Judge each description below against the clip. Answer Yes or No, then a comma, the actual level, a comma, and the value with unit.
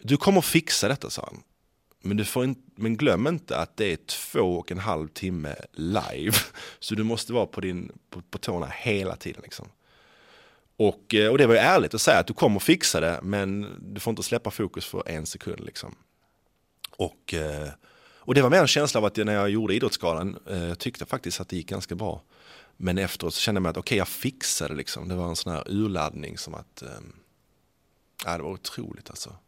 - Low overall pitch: Yes, low, 100 Hz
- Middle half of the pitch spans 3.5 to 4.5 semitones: Yes, average, 4.1 semitones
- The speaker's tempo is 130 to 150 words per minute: No, fast, 205 wpm